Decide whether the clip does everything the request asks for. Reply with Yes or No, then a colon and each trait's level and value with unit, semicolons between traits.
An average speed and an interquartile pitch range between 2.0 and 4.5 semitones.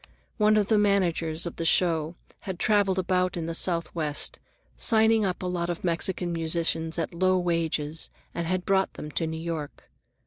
Yes: average, 170 wpm; narrow, 2.4 semitones